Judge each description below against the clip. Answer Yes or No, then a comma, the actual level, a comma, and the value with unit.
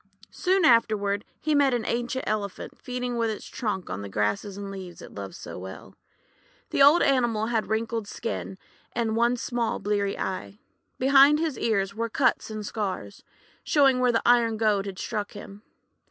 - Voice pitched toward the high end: Yes, high, 220 Hz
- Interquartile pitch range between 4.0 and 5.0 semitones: No, average, 3.6 semitones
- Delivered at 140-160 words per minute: No, average, 175 wpm